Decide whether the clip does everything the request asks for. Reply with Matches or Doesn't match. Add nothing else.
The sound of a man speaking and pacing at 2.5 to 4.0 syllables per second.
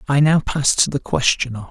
Doesn't match